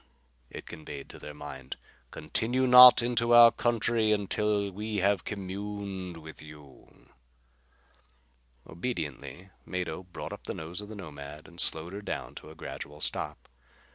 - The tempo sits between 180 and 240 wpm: No, average, 140 wpm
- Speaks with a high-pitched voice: No, very low, 95 Hz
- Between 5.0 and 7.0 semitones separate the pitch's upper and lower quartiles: Yes, wide, 5.4 semitones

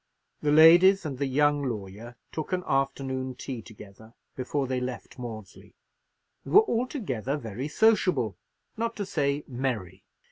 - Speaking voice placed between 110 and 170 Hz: Yes, low, 135 Hz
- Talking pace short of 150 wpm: Yes, average, 140 wpm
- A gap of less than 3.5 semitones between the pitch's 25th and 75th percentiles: No, average, 4.6 semitones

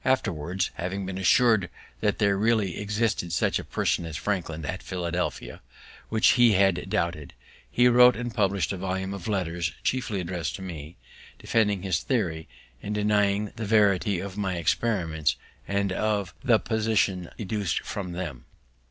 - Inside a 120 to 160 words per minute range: Yes, average, 150 wpm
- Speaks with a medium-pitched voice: No, low, 100 Hz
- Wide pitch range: No, average, 3.3 semitones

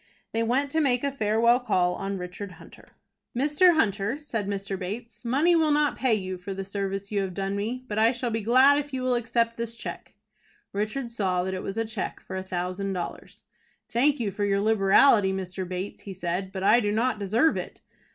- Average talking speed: No, fast, 210 wpm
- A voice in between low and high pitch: No, high, 215 Hz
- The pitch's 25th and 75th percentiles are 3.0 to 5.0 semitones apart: Yes, average, 4.1 semitones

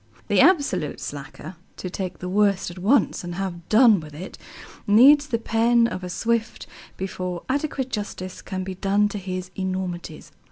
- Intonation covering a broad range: No, average, 4.0 semitones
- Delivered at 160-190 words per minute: Yes, average, 165 wpm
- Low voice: No, high, 190 Hz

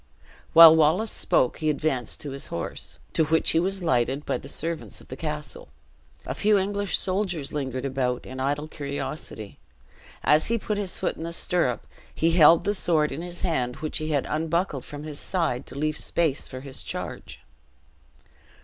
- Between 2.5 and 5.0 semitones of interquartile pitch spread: Yes, average, 3.7 semitones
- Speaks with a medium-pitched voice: Yes, medium, 155 Hz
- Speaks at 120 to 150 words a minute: No, average, 180 wpm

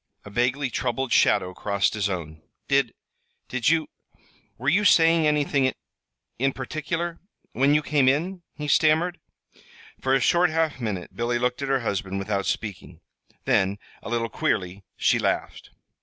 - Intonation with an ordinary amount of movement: No, wide, 6.6 semitones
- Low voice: Yes, low, 130 Hz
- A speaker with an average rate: Yes, average, 155 wpm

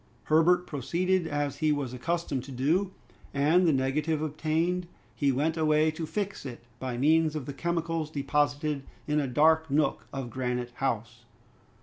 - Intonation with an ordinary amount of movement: Yes, average, 3.1 semitones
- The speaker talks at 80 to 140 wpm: No, average, 155 wpm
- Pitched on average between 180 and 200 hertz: No, medium, 150 Hz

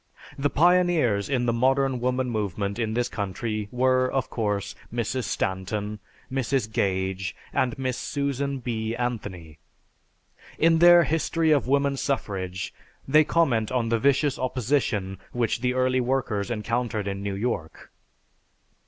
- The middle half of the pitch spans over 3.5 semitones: Yes, average, 4.5 semitones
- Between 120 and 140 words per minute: Yes, slow, 135 wpm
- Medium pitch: No, low, 120 Hz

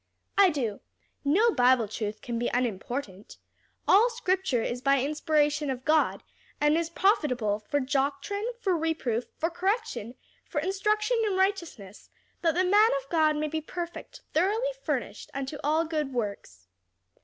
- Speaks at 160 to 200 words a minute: No, average, 145 wpm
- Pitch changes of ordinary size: No, wide, 7.0 semitones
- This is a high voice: Yes, very high, 305 Hz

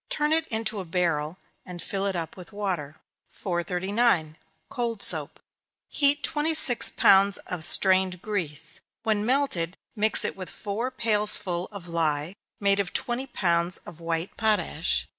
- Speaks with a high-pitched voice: Yes, high, 195 Hz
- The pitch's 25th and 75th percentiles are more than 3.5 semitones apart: Yes, average, 4.3 semitones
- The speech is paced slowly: No, average, 145 wpm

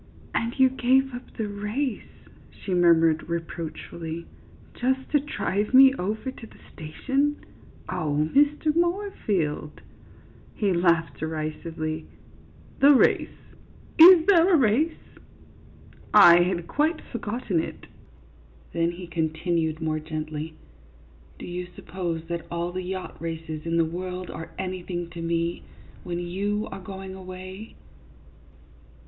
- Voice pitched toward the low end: No, medium, 180 Hz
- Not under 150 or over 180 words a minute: No, slow, 135 wpm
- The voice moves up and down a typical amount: No, wide, 6.5 semitones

